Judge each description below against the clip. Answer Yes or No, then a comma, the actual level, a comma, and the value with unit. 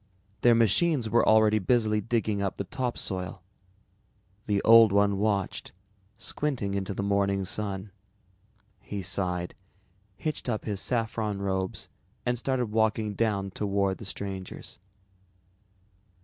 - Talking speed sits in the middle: No, slow, 120 wpm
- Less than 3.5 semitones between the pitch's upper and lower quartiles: Yes, narrow, 2.5 semitones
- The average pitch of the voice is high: No, low, 105 Hz